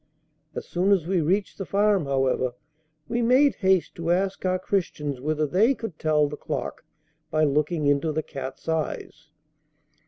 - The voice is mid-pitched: Yes, medium, 165 Hz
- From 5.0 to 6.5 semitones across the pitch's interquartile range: No, average, 4.6 semitones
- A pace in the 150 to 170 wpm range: Yes, average, 160 wpm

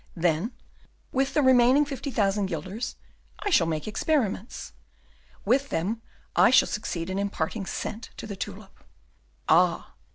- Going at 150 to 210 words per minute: No, slow, 135 wpm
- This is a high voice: Yes, high, 215 Hz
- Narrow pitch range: No, wide, 5.4 semitones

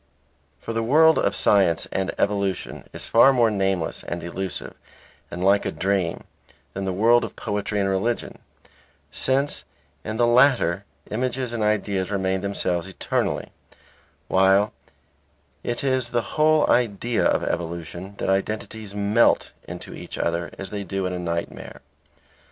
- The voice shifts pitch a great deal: No, average, 3.7 semitones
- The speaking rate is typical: Yes, average, 145 wpm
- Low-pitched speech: Yes, low, 100 Hz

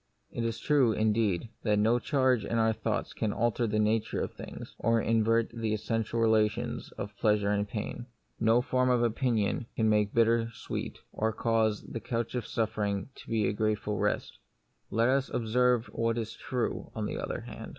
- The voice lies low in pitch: Yes, low, 115 Hz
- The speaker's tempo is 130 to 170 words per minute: No, average, 185 wpm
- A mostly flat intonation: Yes, narrow, 1.6 semitones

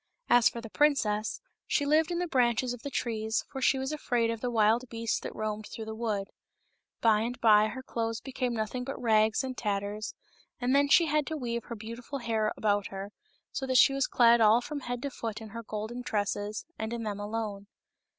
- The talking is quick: Yes, fast, 215 wpm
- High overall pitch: Yes, high, 230 Hz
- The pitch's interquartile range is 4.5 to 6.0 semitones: No, average, 3.0 semitones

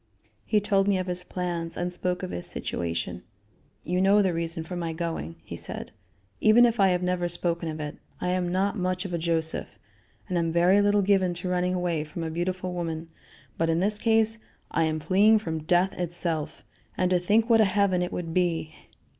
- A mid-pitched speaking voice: Yes, medium, 180 Hz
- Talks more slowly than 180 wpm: No, fast, 205 wpm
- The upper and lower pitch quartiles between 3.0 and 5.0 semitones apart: No, narrow, 2.5 semitones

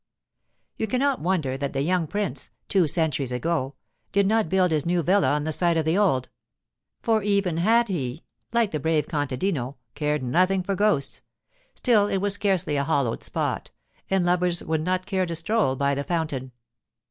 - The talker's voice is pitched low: No, medium, 170 Hz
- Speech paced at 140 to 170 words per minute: No, average, 180 wpm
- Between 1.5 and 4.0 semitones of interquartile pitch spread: No, average, 5.1 semitones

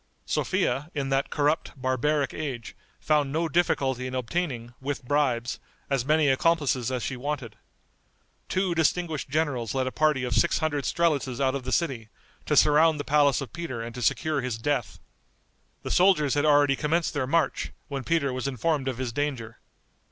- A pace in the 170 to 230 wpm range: Yes, average, 175 wpm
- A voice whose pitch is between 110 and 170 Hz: Yes, medium, 140 Hz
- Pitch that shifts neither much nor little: Yes, average, 3.2 semitones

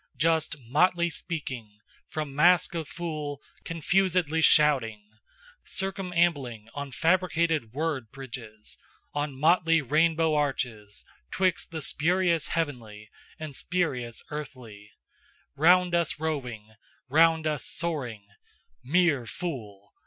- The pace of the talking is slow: Yes, slow, 100 wpm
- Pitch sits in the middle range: Yes, medium, 150 Hz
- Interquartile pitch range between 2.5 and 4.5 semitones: No, average, 5.1 semitones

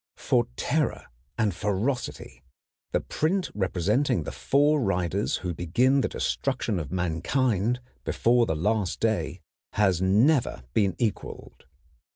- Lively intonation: Yes, wide, 5.7 semitones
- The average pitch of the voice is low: Yes, low, 105 Hz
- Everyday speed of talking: No, slow, 120 wpm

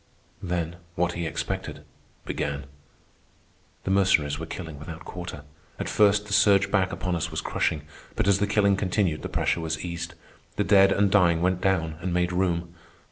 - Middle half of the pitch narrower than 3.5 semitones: Yes, average, 3.0 semitones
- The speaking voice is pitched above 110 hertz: No, very low, 90 Hz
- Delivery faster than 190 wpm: No, average, 175 wpm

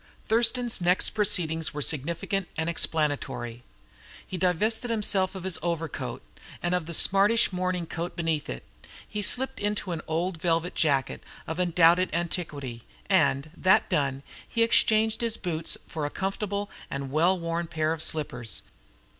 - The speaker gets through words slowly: No, average, 145 wpm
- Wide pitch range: No, average, 3.8 semitones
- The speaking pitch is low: No, medium, 170 Hz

